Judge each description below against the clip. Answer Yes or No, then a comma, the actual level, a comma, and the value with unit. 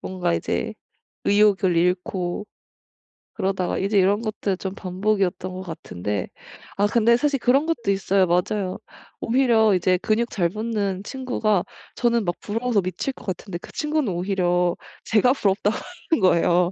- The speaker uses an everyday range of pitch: Yes, average, 3.5 semitones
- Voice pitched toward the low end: No, high, 195 Hz